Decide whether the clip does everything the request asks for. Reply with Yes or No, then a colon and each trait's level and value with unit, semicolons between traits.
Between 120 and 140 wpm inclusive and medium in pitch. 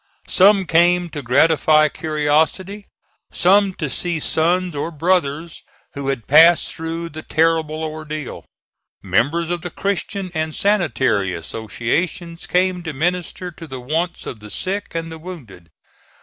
Yes: slow, 135 wpm; medium, 160 Hz